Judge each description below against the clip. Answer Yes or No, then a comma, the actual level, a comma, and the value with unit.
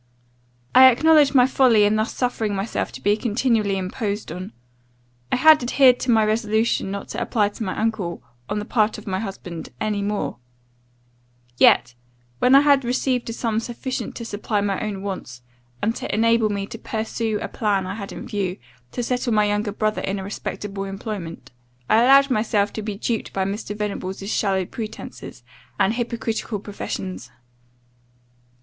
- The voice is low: No, high, 215 Hz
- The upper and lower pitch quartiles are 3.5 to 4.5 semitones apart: No, average, 2.8 semitones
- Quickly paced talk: No, average, 170 wpm